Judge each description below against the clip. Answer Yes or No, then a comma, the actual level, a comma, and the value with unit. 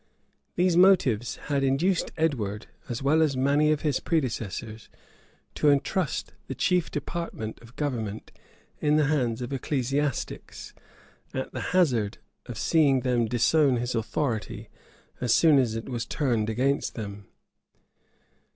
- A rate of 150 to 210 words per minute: No, slow, 135 wpm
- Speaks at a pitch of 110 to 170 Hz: Yes, low, 135 Hz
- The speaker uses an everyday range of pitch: Yes, average, 4.6 semitones